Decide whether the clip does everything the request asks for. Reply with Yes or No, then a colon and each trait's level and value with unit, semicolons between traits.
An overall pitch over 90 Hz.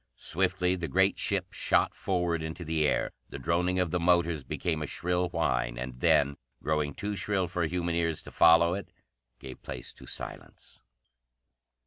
No: very low, 85 Hz